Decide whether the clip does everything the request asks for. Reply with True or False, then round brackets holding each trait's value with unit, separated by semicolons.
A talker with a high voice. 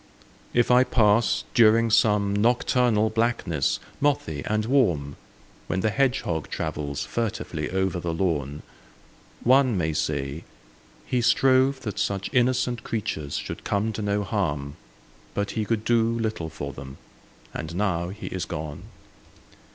False (105 Hz)